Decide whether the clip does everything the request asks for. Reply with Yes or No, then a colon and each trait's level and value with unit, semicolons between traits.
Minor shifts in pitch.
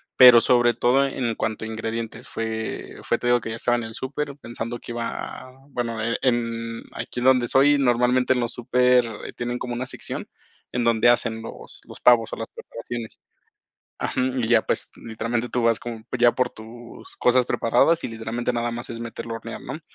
Yes: narrow, 1.4 semitones